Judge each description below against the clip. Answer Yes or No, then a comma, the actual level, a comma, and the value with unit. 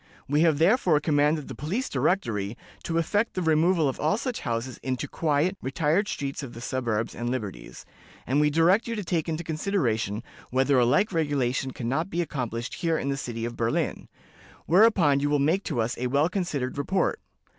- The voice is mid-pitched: Yes, medium, 145 Hz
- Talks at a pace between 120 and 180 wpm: No, average, 190 wpm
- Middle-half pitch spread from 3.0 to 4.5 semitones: No, average, 5.0 semitones